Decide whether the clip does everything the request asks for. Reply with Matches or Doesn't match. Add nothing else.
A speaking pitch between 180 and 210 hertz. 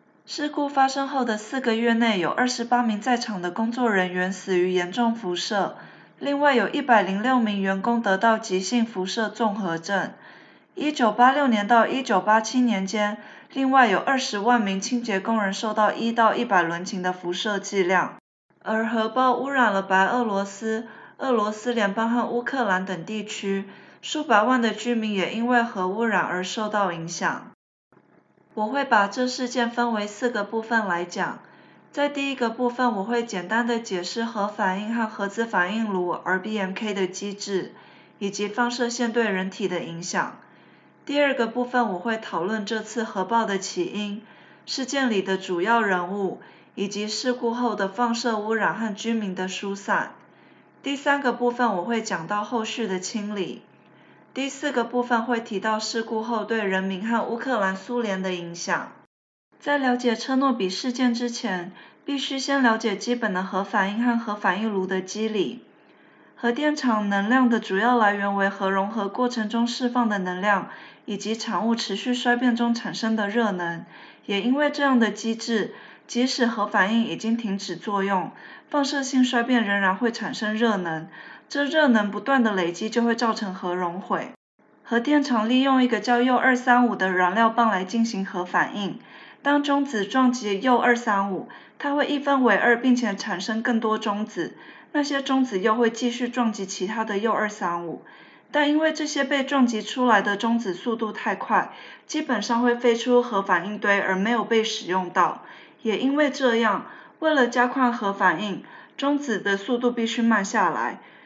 Doesn't match